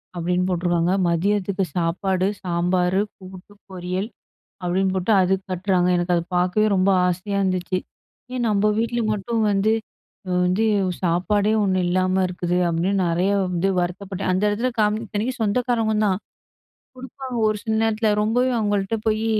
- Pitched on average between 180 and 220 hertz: Yes, high, 190 Hz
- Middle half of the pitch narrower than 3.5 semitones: Yes, average, 2.9 semitones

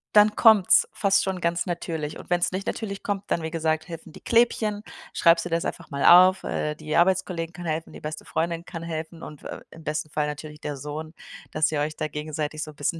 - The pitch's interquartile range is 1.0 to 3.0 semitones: Yes, average, 2.7 semitones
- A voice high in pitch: No, medium, 165 Hz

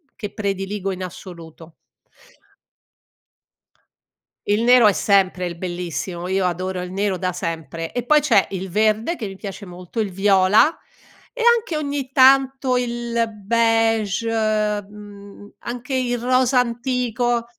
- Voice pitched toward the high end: Yes, high, 210 Hz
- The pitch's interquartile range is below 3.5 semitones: No, average, 4.4 semitones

